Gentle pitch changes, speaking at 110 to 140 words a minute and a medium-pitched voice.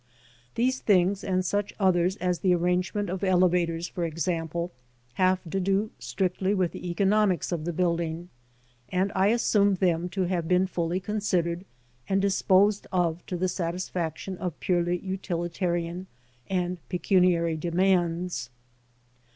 Yes: narrow, 1.8 semitones; slow, 135 wpm; medium, 180 Hz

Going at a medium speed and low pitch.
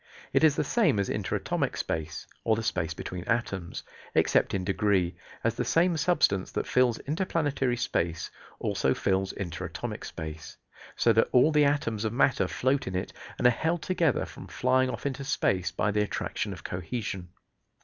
Yes: average, 170 wpm; low, 115 Hz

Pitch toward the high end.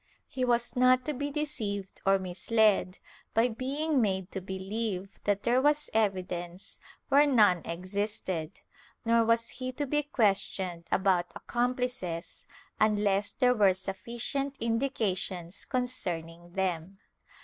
Yes: high, 210 Hz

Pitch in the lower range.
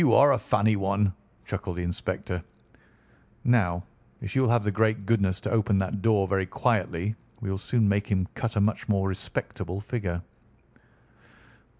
Yes: low, 100 Hz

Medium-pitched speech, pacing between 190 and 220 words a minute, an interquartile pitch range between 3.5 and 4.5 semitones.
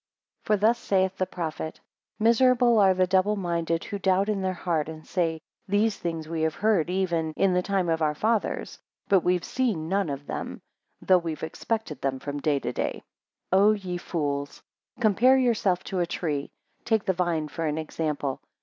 Yes: medium, 180 Hz; average, 195 wpm; average, 4.1 semitones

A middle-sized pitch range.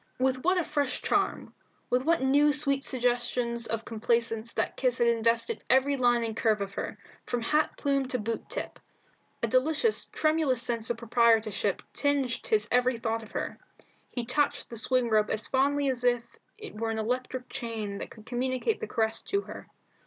Yes: average, 3.0 semitones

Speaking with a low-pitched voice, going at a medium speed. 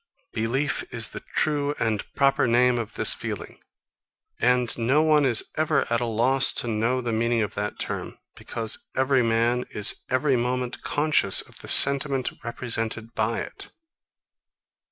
Yes: low, 120 Hz; average, 155 wpm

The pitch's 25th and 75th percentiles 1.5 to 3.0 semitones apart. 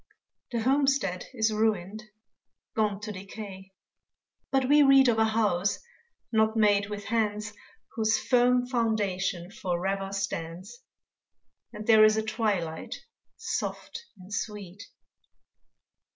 Yes: narrow, 2.6 semitones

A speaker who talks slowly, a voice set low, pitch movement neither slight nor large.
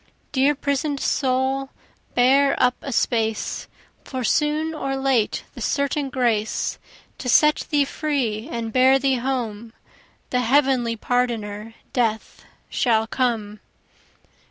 No: slow, 115 wpm; very high, 255 Hz; average, 3.2 semitones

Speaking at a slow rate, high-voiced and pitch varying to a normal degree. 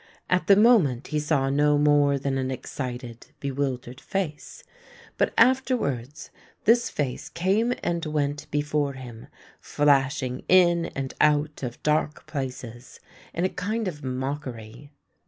No: slow, 130 wpm; medium, 145 Hz; average, 4.1 semitones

